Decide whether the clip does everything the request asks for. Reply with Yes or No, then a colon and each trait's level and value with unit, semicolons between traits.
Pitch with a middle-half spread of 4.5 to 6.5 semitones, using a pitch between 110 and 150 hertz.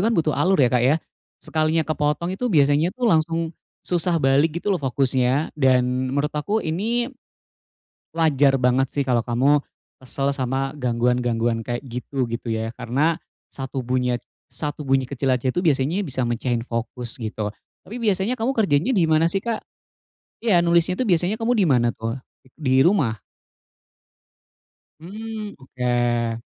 Yes: wide, 5.4 semitones; medium, 140 Hz